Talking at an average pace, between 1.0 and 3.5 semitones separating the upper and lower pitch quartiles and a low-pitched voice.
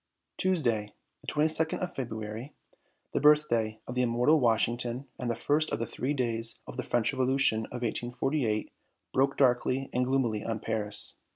Yes: average, 160 wpm; average, 3.2 semitones; low, 125 Hz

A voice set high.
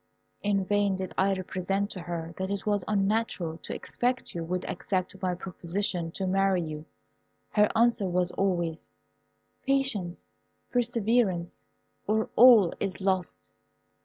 Yes: high, 195 Hz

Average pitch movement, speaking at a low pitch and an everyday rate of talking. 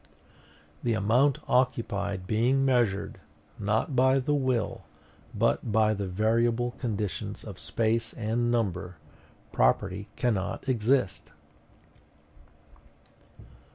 No: average, 3.5 semitones; low, 115 Hz; slow, 90 wpm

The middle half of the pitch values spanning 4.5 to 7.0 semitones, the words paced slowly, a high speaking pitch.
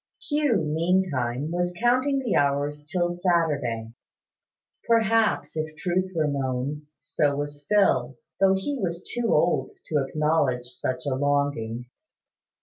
No: average, 4.9 semitones; slow, 130 wpm; medium, 155 Hz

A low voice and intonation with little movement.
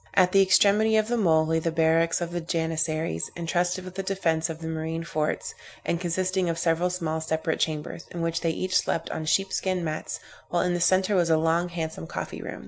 No: medium, 170 Hz; narrow, 2.2 semitones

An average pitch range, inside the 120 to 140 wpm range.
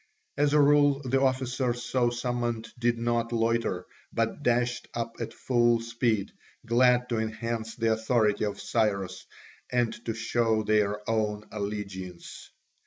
No: narrow, 2.0 semitones; slow, 135 wpm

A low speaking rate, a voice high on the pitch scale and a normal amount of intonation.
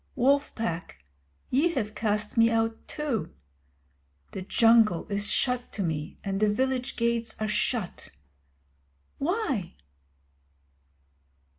Yes: slow, 110 wpm; high, 225 Hz; average, 3.4 semitones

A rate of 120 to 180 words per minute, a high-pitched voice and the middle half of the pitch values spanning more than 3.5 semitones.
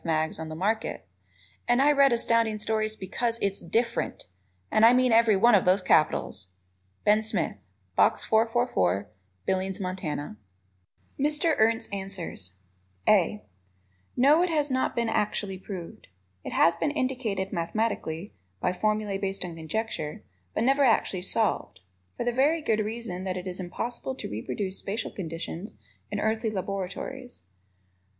Yes: average, 145 wpm; high, 215 Hz; average, 4.3 semitones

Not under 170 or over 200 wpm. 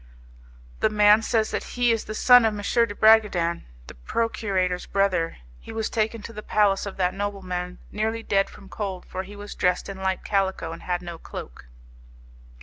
Yes: average, 185 wpm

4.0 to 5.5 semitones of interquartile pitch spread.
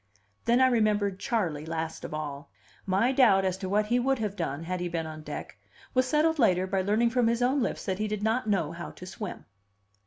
Yes: average, 5.1 semitones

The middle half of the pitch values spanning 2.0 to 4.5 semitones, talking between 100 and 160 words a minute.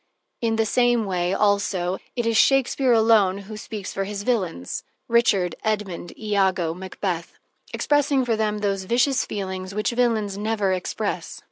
Yes: average, 3.3 semitones; average, 145 wpm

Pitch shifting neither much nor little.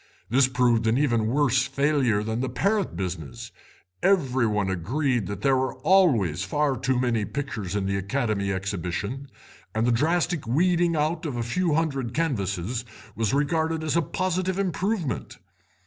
No: wide, 6.6 semitones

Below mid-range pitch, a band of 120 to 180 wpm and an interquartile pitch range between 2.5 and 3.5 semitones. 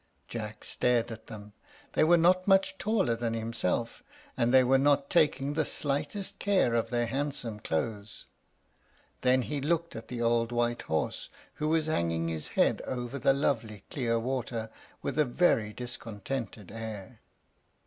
No: low, 120 Hz; average, 155 wpm; average, 4.2 semitones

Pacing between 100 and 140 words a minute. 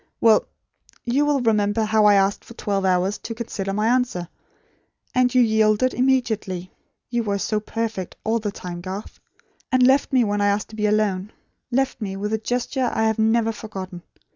No: average, 185 wpm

